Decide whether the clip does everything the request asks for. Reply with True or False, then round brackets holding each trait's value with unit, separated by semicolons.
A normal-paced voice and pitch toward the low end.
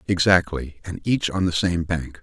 True (190 wpm; 85 Hz)